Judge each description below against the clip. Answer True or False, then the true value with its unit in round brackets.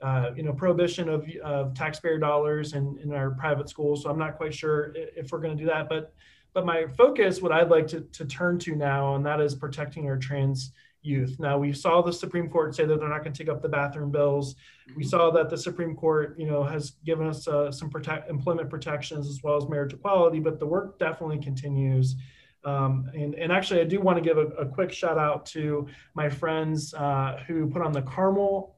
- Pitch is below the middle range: False (155 Hz)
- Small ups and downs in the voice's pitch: True (2.3 semitones)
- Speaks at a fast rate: True (225 wpm)